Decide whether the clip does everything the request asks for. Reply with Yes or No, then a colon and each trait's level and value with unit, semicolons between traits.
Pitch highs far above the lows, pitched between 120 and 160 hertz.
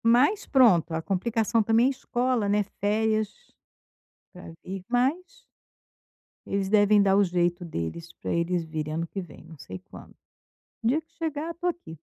No: wide, 6.2 semitones; high, 205 Hz